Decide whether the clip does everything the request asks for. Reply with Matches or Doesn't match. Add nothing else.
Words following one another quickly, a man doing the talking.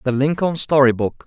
Doesn't match